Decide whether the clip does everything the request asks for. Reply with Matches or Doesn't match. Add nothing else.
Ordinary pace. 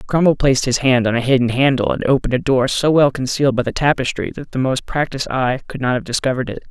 Doesn't match